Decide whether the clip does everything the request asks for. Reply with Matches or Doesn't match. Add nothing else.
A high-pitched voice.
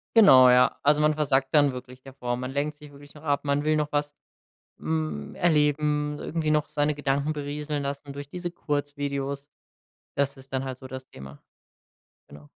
Doesn't match